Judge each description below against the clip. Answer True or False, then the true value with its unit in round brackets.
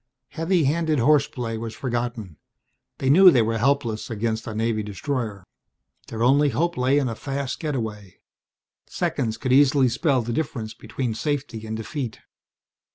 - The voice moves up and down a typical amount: True (4.1 semitones)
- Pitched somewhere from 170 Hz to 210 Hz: False (120 Hz)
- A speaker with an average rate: True (150 wpm)